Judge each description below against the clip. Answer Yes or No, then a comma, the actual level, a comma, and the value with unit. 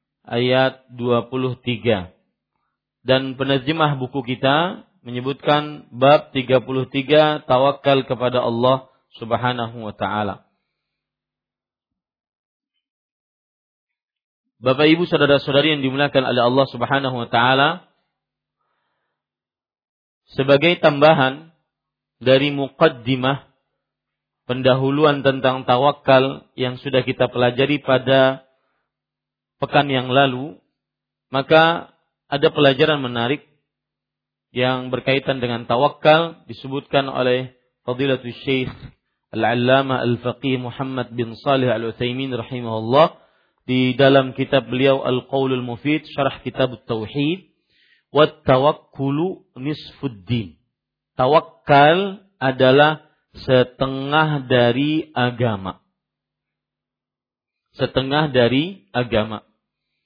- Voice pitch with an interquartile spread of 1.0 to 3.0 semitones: Yes, narrow, 2.5 semitones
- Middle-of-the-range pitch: No, low, 130 Hz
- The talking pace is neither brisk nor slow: No, slow, 80 wpm